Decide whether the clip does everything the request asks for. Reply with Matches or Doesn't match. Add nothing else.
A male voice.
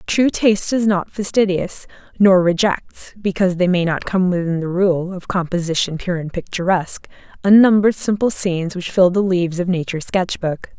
Doesn't match